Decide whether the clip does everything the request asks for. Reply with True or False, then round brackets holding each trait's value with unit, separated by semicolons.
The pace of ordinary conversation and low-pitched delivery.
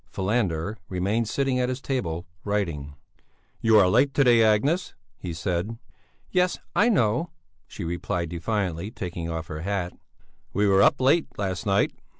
True (155 wpm; 100 Hz)